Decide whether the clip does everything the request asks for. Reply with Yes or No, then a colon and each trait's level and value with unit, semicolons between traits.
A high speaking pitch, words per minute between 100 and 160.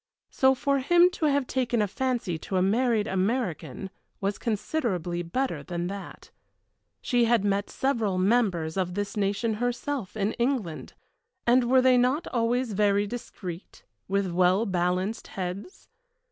Yes: high, 210 Hz; average, 145 wpm